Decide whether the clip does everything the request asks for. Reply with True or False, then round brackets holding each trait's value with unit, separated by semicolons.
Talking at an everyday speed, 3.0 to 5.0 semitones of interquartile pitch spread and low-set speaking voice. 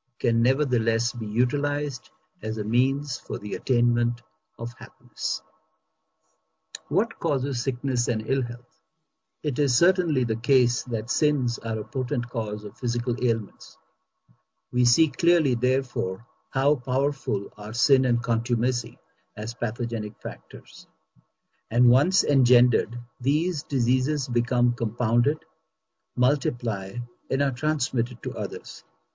False (120 wpm; 2.5 semitones; 125 Hz)